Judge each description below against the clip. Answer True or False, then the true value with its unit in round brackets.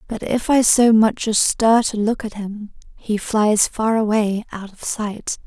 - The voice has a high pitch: True (215 Hz)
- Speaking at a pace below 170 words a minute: False (200 wpm)